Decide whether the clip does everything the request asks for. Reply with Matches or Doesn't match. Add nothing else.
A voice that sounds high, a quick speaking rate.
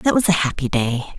Doesn't match